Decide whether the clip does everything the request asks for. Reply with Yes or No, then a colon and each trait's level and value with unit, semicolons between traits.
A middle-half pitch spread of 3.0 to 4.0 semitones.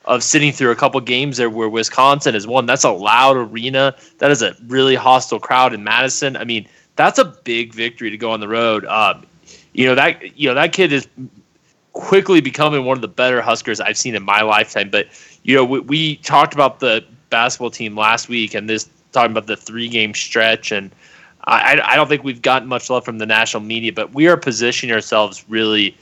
Yes: average, 3.3 semitones